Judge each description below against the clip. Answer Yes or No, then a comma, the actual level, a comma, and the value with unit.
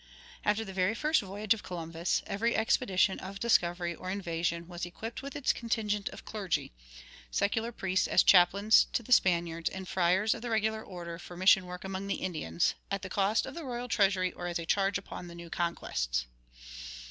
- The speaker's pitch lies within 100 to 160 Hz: No, high, 190 Hz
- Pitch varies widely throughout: No, average, 3.8 semitones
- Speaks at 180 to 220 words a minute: Yes, average, 190 wpm